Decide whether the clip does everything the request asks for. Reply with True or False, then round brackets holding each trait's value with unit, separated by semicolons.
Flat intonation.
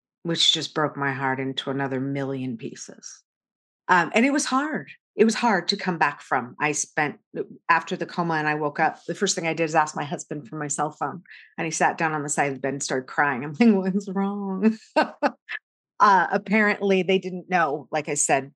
False (4.7 semitones)